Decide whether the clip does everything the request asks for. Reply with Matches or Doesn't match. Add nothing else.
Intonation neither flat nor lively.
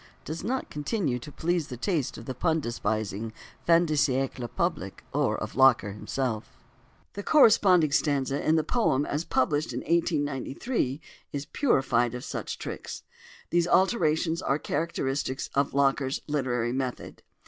Matches